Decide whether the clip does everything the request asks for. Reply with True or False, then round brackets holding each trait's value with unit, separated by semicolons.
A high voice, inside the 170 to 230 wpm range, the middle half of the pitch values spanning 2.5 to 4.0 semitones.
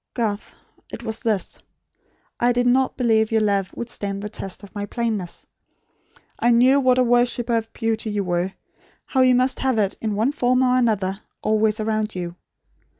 True (225 Hz; 180 wpm; 3.2 semitones)